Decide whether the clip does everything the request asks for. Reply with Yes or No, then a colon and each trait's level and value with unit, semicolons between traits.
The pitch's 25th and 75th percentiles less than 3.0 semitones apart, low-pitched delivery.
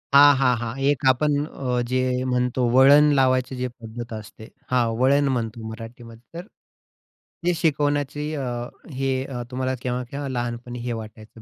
Yes: narrow, 2.6 semitones; low, 125 Hz